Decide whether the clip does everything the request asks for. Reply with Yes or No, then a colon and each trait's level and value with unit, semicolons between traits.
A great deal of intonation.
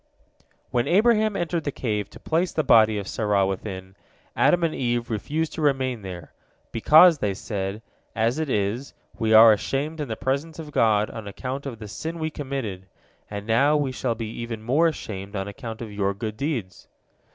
Yes: wide, 6.0 semitones